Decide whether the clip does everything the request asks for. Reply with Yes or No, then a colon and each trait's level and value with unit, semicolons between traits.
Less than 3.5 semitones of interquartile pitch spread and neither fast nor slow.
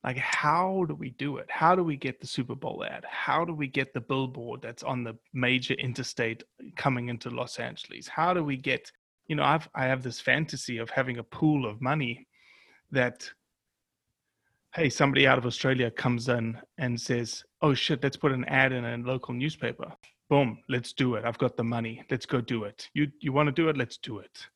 No: average, 2.7 semitones; fast, 215 wpm